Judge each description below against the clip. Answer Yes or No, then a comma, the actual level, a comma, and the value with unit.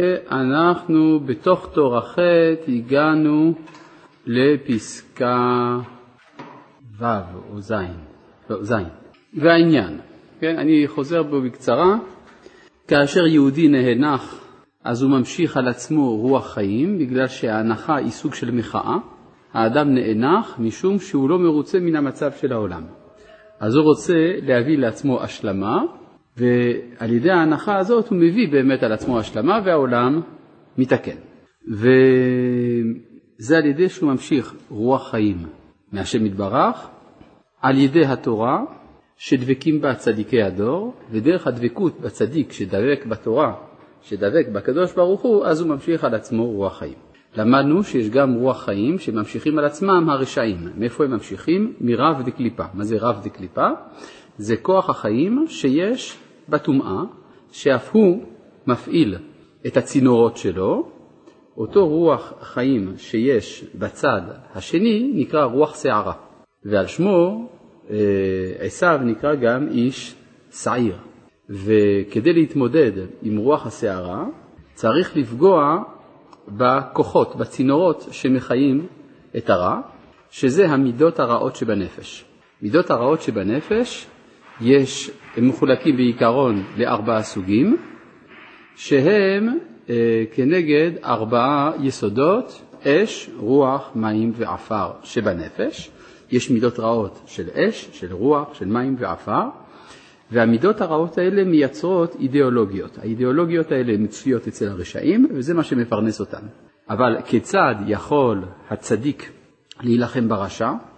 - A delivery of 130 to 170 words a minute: No, average, 110 wpm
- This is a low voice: Yes, low, 130 Hz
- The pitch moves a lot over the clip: Yes, wide, 5.9 semitones